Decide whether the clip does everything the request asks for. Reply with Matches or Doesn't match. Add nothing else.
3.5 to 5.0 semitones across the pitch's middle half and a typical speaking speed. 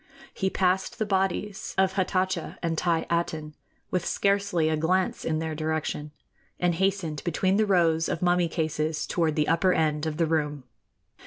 Doesn't match